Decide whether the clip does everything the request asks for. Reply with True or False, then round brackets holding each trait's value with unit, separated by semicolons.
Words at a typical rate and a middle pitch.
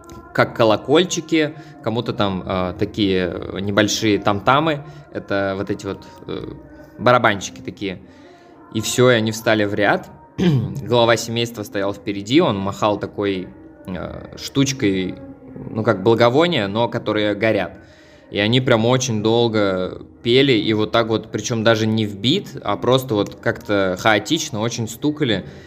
False (135 wpm; 110 Hz)